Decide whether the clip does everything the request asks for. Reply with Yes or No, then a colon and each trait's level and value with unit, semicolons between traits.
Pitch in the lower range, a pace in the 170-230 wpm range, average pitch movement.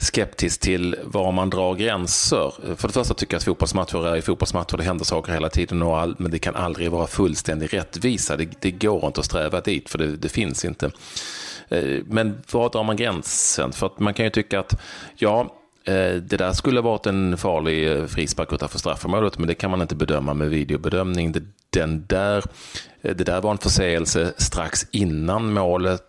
Yes: very low, 90 Hz; average, 190 wpm; average, 3.5 semitones